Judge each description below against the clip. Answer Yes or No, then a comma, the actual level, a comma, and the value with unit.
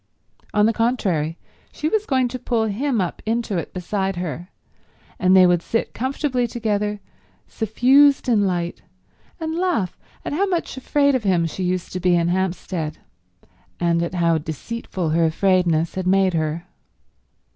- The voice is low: No, high, 190 Hz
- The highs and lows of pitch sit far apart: Yes, wide, 5.8 semitones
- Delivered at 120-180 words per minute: Yes, average, 155 wpm